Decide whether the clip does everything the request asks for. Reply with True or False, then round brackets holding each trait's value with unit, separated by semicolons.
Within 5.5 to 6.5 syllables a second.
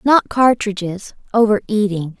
False (4.4 syllables/s)